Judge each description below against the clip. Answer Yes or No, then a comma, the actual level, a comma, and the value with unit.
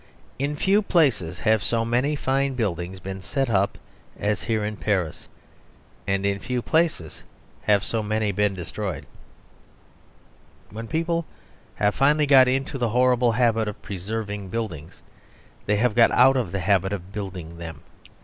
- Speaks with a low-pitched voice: Yes, low, 110 Hz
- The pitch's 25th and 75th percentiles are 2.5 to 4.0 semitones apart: No, average, 4.7 semitones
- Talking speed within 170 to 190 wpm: No, average, 155 wpm